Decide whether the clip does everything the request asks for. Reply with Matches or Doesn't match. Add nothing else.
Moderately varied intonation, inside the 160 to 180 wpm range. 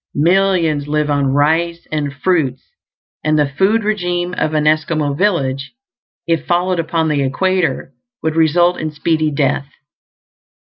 Doesn't match